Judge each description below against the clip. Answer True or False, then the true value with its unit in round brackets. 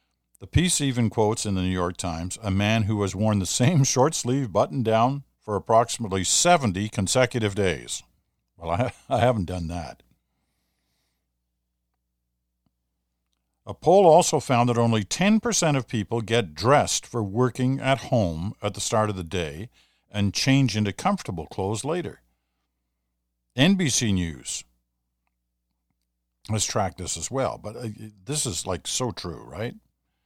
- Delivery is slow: False (145 wpm)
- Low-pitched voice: True (100 Hz)